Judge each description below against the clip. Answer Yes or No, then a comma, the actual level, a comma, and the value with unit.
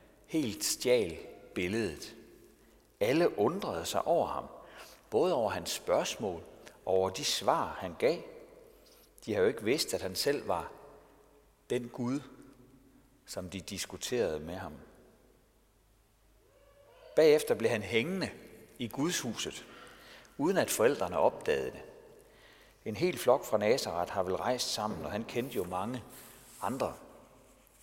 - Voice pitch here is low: No, medium, 160 Hz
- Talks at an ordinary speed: No, slow, 130 wpm